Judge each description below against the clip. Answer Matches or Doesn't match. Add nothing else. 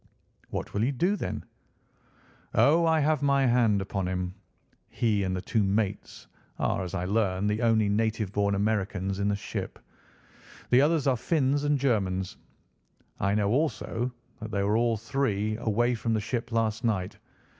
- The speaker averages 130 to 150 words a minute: Doesn't match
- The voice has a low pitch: Matches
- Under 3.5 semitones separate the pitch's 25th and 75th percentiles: Doesn't match